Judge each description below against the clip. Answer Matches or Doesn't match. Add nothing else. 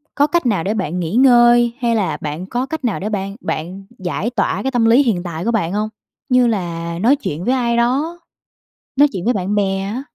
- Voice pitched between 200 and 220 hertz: Matches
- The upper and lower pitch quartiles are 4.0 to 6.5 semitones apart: Matches